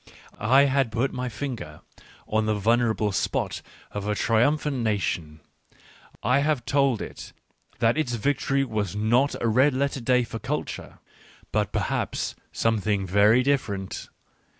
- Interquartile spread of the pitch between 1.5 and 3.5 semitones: No, average, 4.4 semitones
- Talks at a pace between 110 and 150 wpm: Yes, average, 140 wpm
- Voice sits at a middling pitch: No, low, 120 Hz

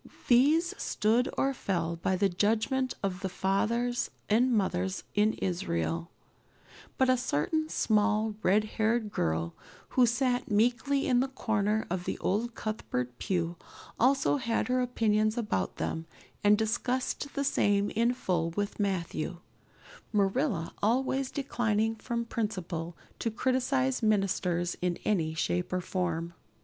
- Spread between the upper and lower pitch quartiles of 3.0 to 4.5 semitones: No, average, 5.1 semitones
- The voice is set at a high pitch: Yes, high, 215 Hz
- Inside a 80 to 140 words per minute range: Yes, slow, 135 wpm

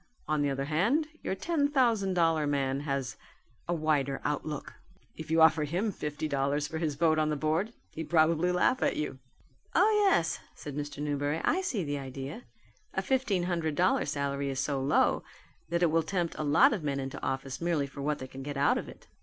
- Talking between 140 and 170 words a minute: No, fast, 205 wpm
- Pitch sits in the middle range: Yes, medium, 155 Hz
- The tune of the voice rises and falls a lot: No, average, 3.6 semitones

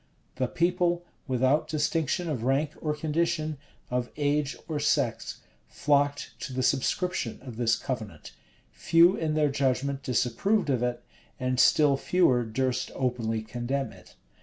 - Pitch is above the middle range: No, medium, 140 Hz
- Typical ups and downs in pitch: Yes, average, 3.7 semitones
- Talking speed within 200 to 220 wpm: No, average, 140 wpm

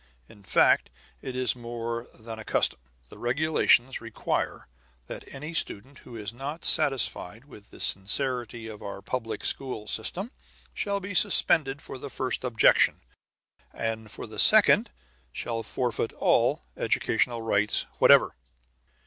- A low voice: Yes, low, 120 Hz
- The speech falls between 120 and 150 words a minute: Yes, slow, 135 wpm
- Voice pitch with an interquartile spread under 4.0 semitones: Yes, average, 3.3 semitones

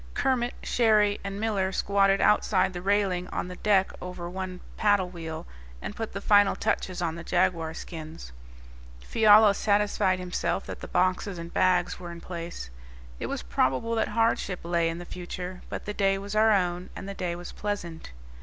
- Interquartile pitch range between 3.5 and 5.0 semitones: No, average, 2.7 semitones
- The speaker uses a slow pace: No, average, 180 wpm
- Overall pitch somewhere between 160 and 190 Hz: Yes, medium, 185 Hz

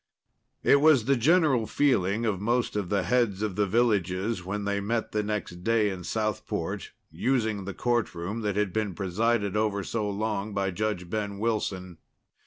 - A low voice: Yes, low, 105 Hz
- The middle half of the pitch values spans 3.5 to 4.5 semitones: No, average, 2.7 semitones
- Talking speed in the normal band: Yes, average, 170 wpm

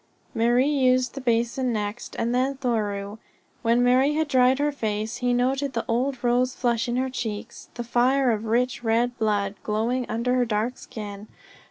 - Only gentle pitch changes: Yes, narrow, 2.3 semitones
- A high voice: Yes, high, 245 Hz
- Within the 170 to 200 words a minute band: Yes, average, 175 wpm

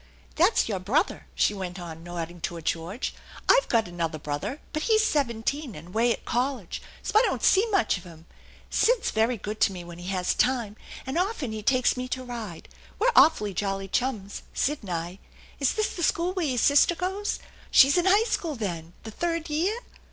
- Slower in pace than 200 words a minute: No, fast, 205 wpm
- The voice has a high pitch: Yes, high, 235 Hz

